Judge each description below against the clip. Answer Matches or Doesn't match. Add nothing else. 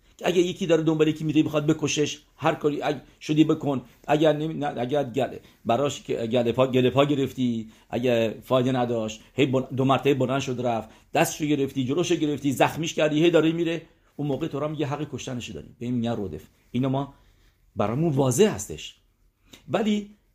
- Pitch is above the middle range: Doesn't match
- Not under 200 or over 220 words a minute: Doesn't match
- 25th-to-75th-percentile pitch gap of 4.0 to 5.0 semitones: Matches